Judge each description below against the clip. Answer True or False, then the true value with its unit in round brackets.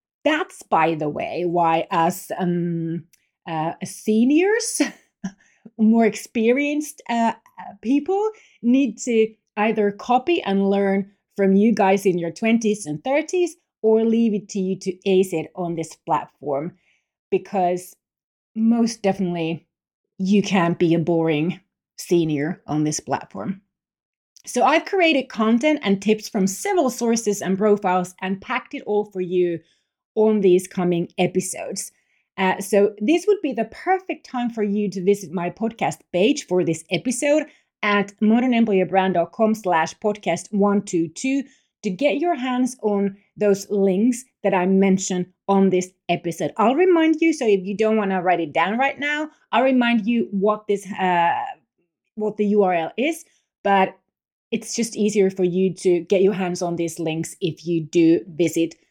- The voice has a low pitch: False (200 Hz)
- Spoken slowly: False (150 wpm)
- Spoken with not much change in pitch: False (4.4 semitones)